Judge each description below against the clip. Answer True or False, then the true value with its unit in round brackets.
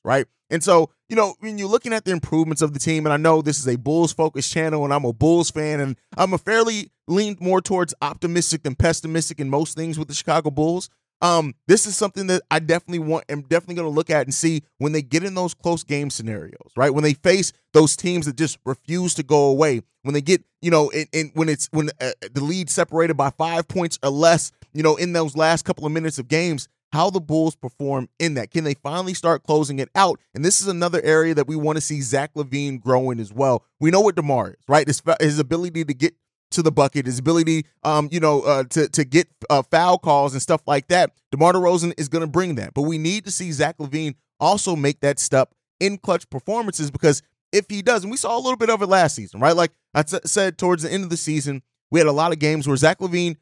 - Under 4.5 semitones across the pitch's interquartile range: True (3.1 semitones)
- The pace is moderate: False (250 wpm)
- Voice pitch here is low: False (160 Hz)